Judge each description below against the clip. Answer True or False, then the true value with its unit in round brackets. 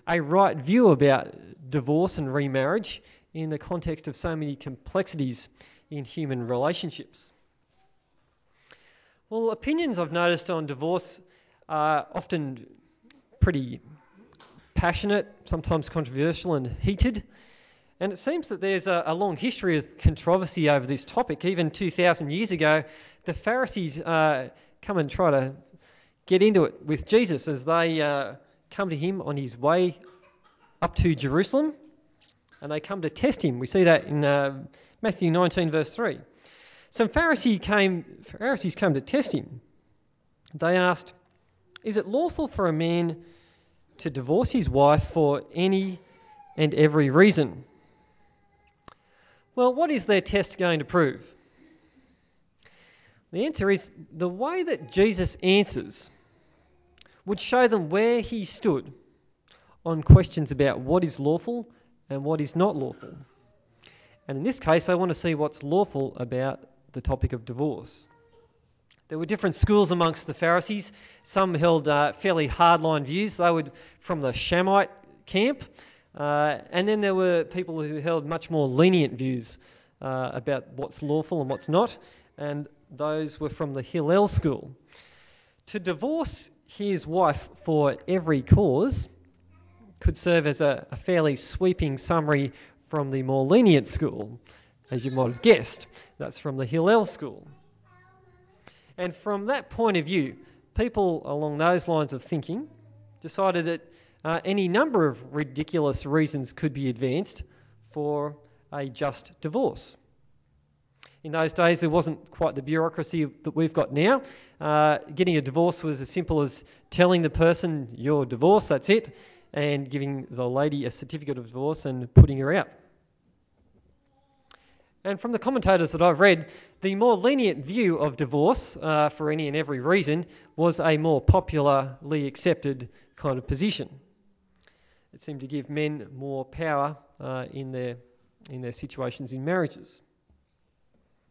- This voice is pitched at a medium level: True (160 Hz)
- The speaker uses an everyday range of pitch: True (4.5 semitones)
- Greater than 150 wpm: False (145 wpm)